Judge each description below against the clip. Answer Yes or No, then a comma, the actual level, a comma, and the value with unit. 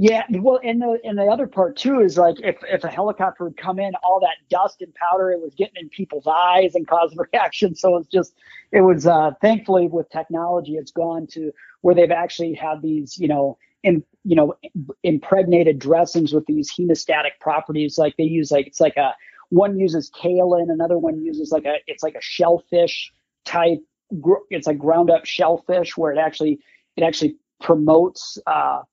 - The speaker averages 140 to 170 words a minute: No, average, 195 wpm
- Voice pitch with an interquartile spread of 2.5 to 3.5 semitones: Yes, average, 2.8 semitones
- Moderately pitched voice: Yes, medium, 170 Hz